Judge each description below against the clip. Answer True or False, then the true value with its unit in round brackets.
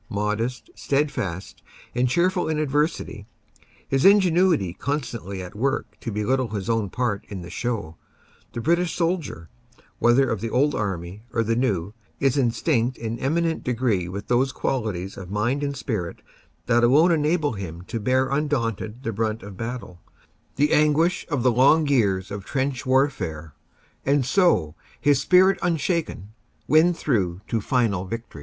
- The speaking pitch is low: True (120 Hz)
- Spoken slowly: False (150 wpm)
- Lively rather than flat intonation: True (6.0 semitones)